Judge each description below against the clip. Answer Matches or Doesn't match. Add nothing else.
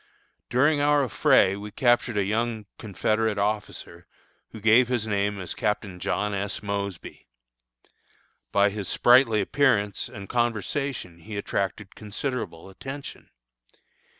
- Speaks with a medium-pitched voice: Doesn't match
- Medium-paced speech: Doesn't match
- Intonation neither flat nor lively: Matches